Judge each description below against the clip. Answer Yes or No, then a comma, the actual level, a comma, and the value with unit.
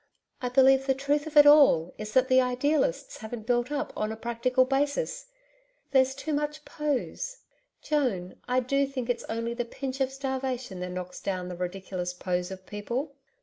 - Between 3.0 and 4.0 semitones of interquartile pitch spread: No, average, 4.7 semitones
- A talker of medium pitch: No, very high, 255 Hz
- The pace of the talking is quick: No, average, 180 wpm